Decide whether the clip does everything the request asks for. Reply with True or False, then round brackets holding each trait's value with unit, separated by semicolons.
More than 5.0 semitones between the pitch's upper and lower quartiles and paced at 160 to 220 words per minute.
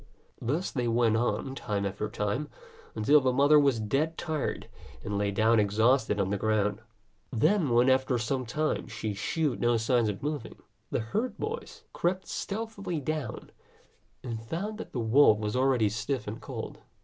True (5.6 semitones; 165 wpm)